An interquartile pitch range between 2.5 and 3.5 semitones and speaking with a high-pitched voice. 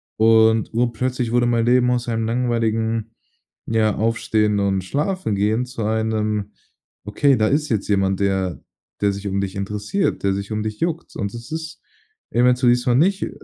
No: average, 2.9 semitones; low, 110 Hz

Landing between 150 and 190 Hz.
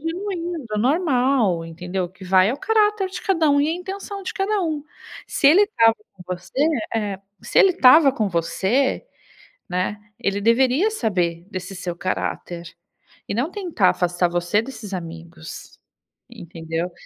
No: high, 225 Hz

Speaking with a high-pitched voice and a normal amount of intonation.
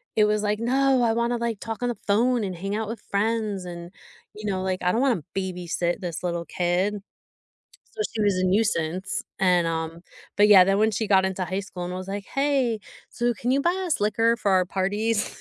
Yes: high, 205 Hz; average, 3.7 semitones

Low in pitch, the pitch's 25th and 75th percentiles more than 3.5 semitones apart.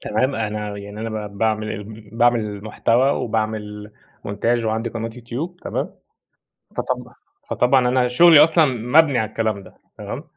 No: low, 115 Hz; narrow, 2.6 semitones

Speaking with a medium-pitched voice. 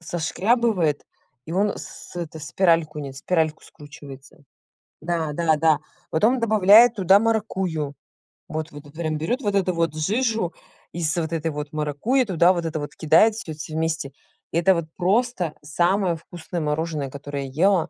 Yes: medium, 165 Hz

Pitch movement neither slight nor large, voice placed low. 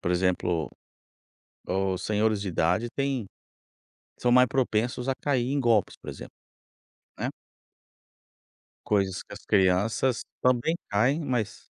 Yes: average, 4.9 semitones; low, 110 Hz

